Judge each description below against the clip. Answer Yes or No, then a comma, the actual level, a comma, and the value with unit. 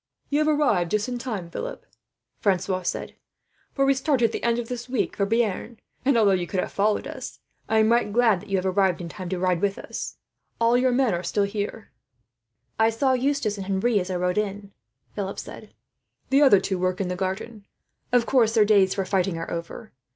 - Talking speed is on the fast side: Yes, fast, 220 wpm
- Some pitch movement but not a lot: Yes, average, 4.2 semitones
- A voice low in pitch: No, high, 210 Hz